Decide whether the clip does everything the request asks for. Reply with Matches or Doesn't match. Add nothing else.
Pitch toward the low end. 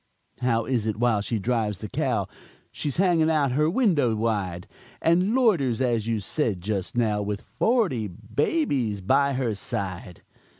Matches